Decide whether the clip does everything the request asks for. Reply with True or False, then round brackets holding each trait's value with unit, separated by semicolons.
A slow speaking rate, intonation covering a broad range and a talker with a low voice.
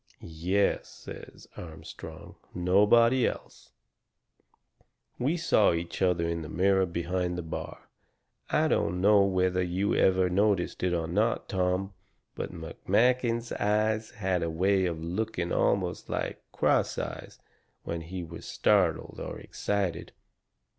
False (125 wpm; 3.1 semitones; 95 Hz)